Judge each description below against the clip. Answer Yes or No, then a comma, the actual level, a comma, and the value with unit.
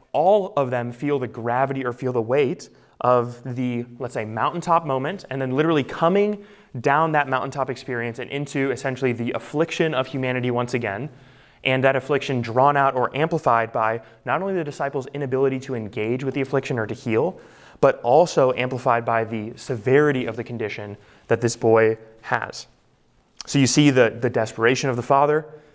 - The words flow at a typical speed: Yes, average, 175 wpm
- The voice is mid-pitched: No, low, 130 Hz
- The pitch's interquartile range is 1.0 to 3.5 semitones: Yes, average, 3.0 semitones